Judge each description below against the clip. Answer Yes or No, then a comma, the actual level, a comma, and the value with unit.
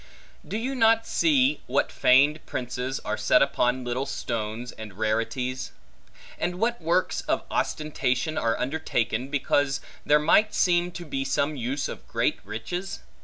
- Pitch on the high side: No, medium, 140 Hz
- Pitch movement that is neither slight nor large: No, wide, 6.0 semitones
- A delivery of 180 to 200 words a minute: No, average, 145 wpm